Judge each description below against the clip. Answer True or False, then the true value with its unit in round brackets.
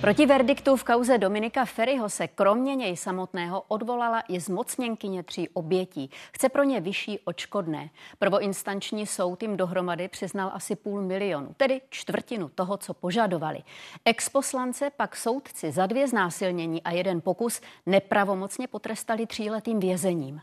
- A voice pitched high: True (200 Hz)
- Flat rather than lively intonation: False (4.0 semitones)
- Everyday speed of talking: True (135 wpm)